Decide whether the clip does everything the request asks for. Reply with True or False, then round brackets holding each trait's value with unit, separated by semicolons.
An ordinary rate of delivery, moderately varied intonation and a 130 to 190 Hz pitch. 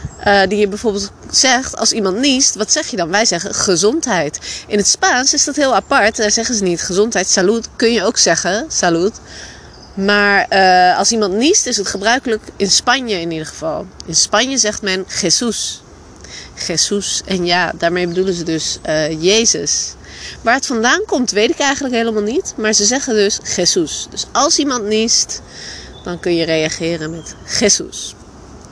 False (175 wpm; 4.5 semitones; 205 Hz)